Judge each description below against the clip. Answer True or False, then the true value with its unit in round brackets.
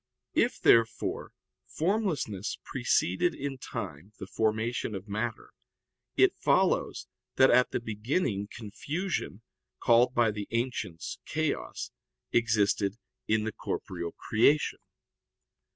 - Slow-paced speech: True (105 wpm)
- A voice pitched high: False (110 Hz)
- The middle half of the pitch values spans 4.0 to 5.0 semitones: False (3.6 semitones)